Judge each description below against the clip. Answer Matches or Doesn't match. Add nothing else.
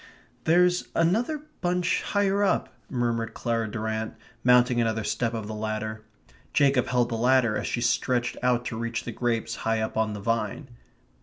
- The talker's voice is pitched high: Doesn't match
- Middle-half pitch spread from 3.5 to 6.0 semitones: Doesn't match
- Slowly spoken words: Doesn't match